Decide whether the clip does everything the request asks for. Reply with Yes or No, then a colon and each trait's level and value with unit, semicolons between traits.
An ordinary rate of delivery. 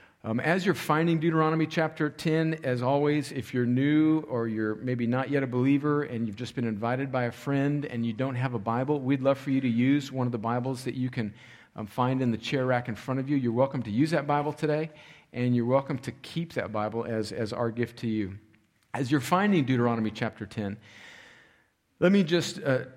No: fast, 225 wpm